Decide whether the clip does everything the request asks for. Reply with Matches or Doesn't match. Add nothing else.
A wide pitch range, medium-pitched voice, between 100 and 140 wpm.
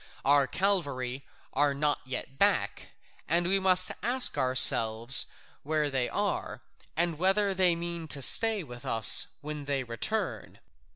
Matches